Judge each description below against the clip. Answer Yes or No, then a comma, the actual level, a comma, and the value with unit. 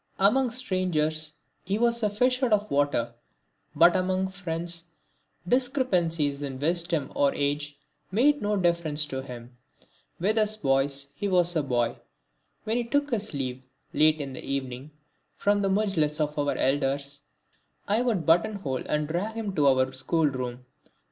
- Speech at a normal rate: Yes, average, 155 wpm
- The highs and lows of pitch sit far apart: Yes, wide, 6.5 semitones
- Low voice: No, medium, 165 Hz